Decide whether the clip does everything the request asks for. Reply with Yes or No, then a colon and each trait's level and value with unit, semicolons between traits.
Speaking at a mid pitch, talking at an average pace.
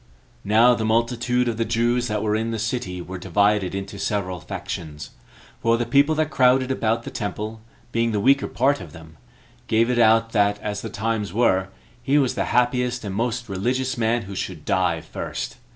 No: low, 115 Hz; average, 190 wpm